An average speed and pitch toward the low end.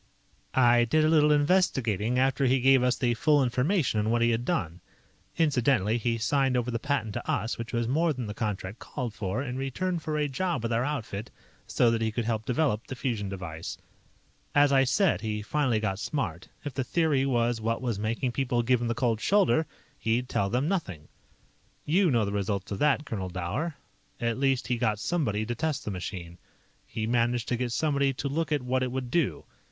No: fast, 210 wpm; low, 125 Hz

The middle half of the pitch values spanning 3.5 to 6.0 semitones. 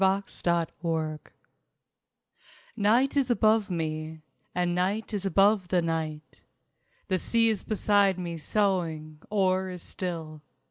Yes: average, 3.8 semitones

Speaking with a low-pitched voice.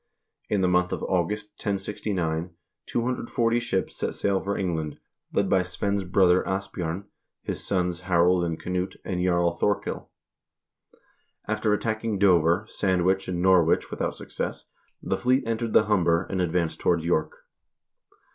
Yes: very low, 95 Hz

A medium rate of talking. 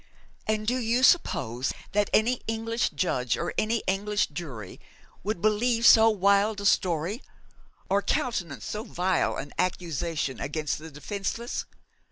No: slow, 130 wpm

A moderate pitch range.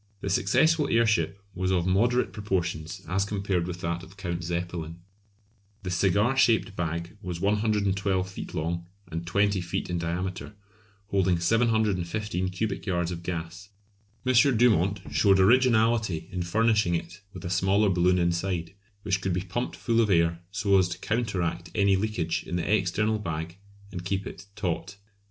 Yes: average, 3.3 semitones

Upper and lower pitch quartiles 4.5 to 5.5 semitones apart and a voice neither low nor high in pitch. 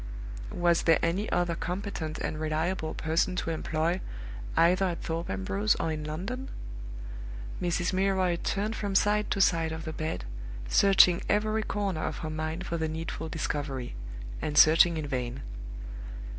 No: average, 3.2 semitones; medium, 165 Hz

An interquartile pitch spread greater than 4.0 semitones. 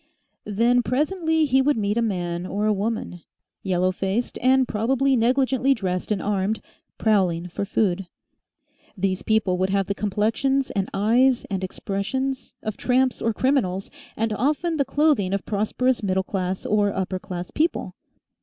Yes: average, 5.2 semitones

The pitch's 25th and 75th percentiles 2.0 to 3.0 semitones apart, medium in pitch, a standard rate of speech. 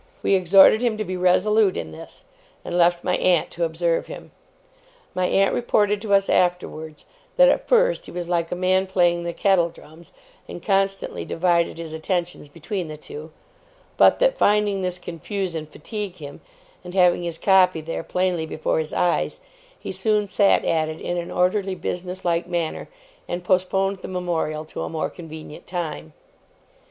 Yes: narrow, 2.6 semitones; medium, 180 Hz; average, 175 wpm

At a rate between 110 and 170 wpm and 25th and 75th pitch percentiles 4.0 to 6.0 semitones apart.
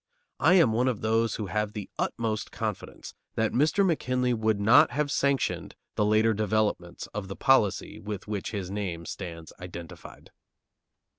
No: average, 155 wpm; average, 3.5 semitones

